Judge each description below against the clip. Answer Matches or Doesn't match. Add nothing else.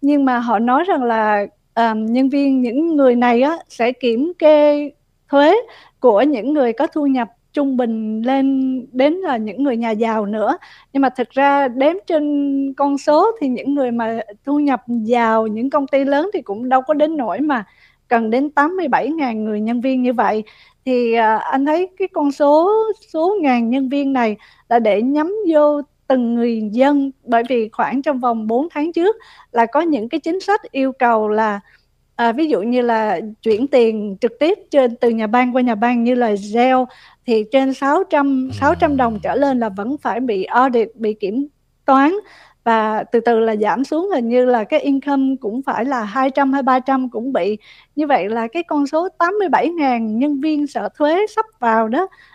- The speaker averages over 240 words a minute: Doesn't match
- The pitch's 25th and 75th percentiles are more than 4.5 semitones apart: Doesn't match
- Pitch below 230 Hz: Doesn't match